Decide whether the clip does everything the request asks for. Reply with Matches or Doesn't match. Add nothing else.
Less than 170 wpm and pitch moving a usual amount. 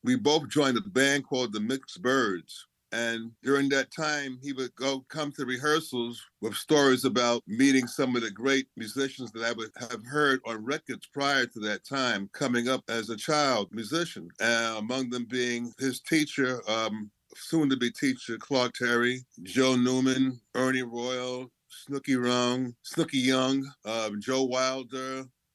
Doesn't match